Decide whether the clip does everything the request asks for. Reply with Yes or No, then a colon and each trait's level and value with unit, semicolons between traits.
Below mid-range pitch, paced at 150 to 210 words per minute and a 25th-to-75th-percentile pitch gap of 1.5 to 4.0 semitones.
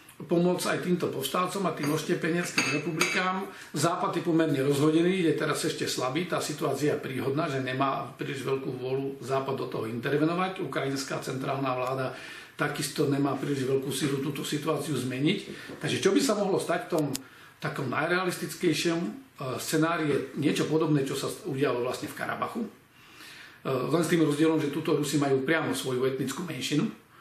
No: medium, 150 Hz; average, 160 wpm; average, 3.6 semitones